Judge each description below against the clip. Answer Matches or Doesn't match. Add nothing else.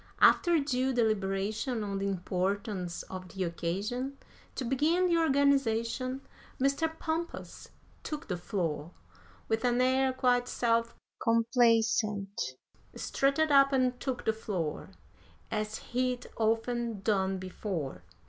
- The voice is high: Matches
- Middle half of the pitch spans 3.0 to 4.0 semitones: Doesn't match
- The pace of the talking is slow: Matches